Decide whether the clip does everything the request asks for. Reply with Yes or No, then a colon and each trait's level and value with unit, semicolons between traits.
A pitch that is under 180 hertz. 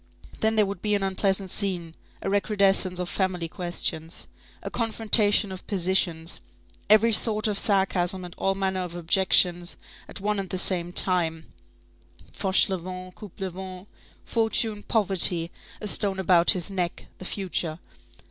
No: high, 190 Hz